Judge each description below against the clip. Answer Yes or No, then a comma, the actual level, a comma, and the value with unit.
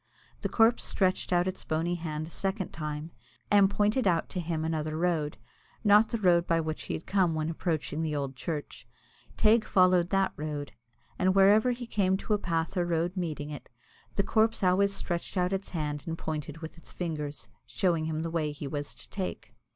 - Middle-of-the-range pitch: Yes, medium, 170 Hz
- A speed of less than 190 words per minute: No, average, 195 wpm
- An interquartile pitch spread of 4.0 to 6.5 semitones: No, average, 3.6 semitones